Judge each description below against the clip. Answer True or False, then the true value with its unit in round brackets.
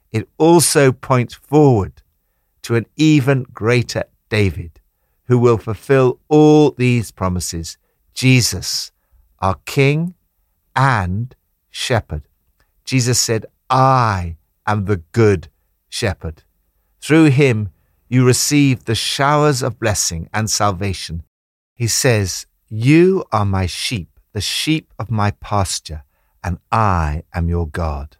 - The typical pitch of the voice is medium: False (105 Hz)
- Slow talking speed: True (115 wpm)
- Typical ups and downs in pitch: False (7.1 semitones)